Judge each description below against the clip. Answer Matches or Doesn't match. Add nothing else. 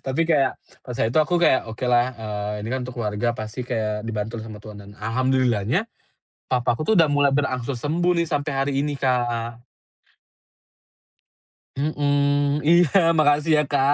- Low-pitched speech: Matches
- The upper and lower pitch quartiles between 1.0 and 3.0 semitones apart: Doesn't match